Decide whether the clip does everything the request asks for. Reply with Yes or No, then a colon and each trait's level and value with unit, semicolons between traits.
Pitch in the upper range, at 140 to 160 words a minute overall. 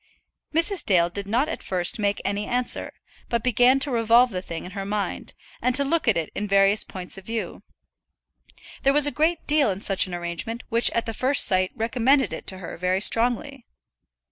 No: high, 225 Hz; average, 200 wpm